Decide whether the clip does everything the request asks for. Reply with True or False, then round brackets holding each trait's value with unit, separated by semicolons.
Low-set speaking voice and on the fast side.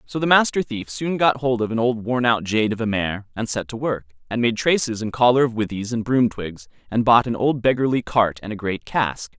True (115 Hz; 255 wpm)